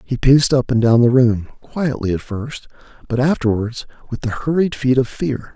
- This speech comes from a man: Yes, male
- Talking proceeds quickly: No, average, 195 wpm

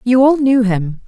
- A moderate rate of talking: No, fast, 225 wpm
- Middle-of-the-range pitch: No, high, 235 Hz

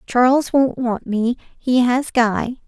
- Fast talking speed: No, average, 155 wpm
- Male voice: No, female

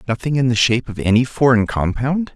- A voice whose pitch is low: Yes, low, 125 Hz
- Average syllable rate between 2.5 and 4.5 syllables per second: No, 6.0 syllables/s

